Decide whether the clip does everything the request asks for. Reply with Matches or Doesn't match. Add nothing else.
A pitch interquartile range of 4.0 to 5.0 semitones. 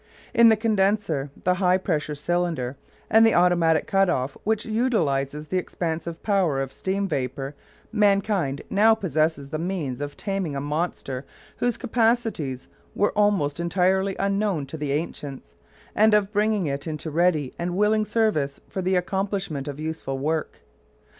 Doesn't match